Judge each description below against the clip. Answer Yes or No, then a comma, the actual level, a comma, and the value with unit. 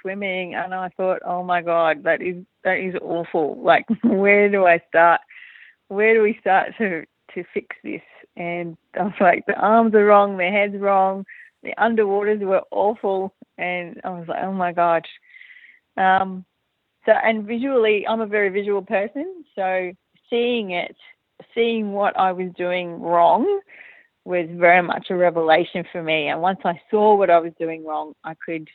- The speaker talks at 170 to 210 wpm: Yes, average, 175 wpm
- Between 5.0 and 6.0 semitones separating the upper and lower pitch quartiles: No, average, 3.5 semitones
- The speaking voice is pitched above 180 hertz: Yes, high, 190 Hz